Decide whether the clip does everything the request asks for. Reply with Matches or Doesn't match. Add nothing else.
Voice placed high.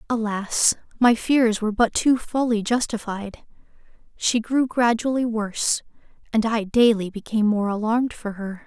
Matches